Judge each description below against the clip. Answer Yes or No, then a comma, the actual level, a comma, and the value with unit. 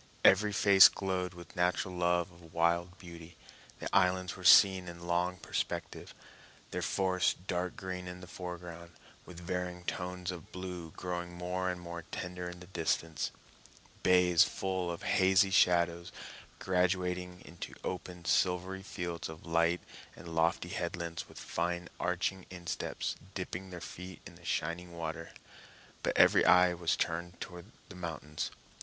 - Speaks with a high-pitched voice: No, very low, 90 Hz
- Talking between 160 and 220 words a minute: No, average, 145 wpm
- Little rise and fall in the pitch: Yes, narrow, 1.1 semitones